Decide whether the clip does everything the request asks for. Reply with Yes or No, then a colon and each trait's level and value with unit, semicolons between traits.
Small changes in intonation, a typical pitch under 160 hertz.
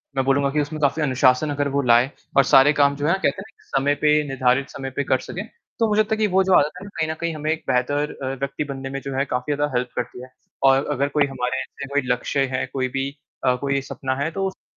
Yes: narrow, 2.2 semitones; medium, 140 Hz